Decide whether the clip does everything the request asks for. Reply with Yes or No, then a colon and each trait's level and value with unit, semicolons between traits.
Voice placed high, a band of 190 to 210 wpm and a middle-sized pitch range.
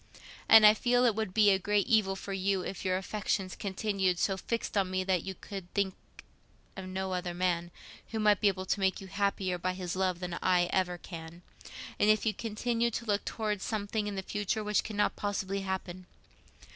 No: high, 195 Hz; fast, 205 wpm; narrow, 2.2 semitones